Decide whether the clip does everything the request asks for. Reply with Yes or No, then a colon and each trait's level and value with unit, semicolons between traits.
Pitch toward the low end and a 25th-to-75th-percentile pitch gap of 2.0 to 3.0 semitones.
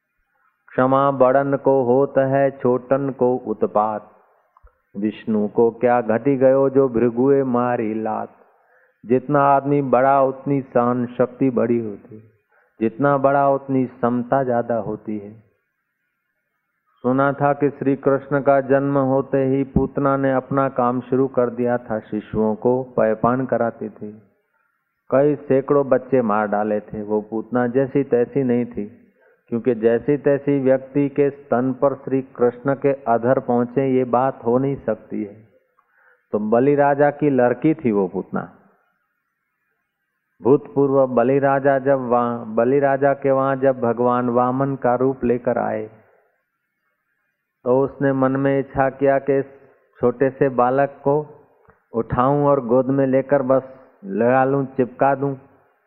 Yes: low, 130 Hz; narrow, 2.5 semitones